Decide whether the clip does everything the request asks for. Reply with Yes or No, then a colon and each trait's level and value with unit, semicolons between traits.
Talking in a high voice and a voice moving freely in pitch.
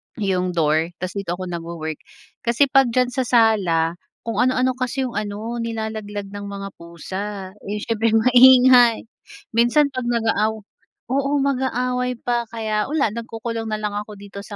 No: high, 225 Hz; average, 3.7 semitones